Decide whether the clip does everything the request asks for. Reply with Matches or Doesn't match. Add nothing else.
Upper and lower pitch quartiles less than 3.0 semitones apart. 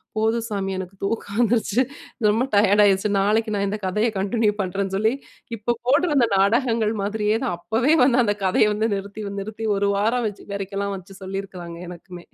Matches